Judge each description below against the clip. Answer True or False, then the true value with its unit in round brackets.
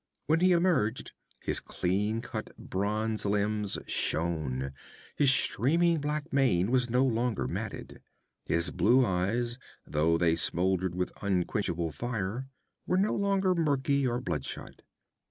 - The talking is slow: True (125 wpm)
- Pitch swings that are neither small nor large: False (7.1 semitones)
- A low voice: True (110 Hz)